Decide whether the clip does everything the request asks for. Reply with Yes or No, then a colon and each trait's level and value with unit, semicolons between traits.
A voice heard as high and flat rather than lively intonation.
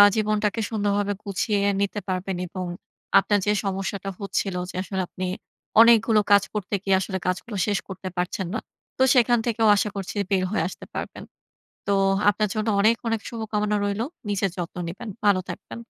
Yes: high, 205 Hz; narrow, 2.0 semitones